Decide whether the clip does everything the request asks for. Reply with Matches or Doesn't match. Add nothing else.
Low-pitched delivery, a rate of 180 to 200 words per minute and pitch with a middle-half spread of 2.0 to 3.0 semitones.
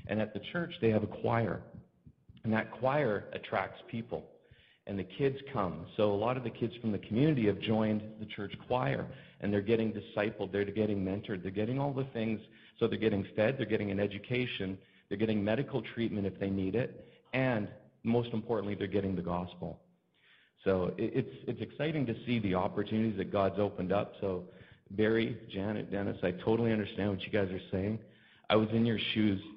Matches